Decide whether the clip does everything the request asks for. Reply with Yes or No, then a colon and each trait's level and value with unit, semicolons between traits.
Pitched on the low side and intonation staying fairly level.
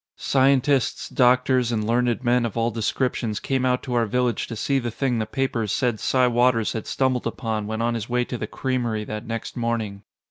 Yes: low, 120 Hz; narrow, 2.1 semitones